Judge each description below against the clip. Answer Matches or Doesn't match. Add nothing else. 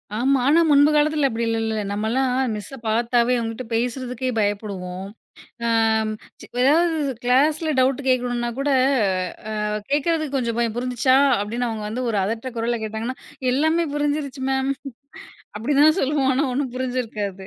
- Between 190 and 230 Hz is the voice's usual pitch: Doesn't match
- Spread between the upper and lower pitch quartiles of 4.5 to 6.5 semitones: Doesn't match